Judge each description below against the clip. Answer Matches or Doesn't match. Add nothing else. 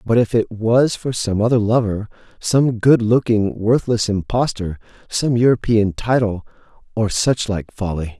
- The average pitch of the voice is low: Matches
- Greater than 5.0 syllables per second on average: Doesn't match